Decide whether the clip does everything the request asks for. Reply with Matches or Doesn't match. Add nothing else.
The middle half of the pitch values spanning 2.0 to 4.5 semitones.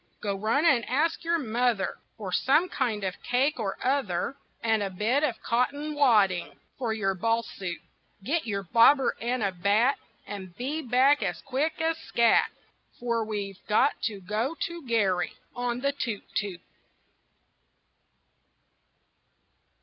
Doesn't match